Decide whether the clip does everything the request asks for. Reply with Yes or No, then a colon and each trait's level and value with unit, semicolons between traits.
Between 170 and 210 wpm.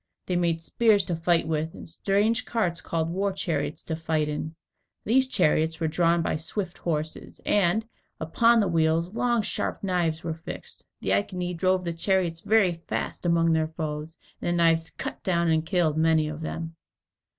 Yes: average, 175 wpm